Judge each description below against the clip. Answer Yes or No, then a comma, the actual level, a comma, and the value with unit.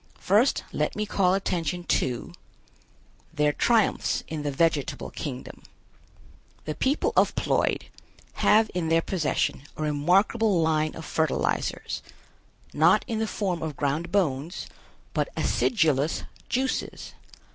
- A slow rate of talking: Yes, slow, 120 wpm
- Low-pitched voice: No, medium, 165 Hz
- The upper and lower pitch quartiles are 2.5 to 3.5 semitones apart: No, average, 4.9 semitones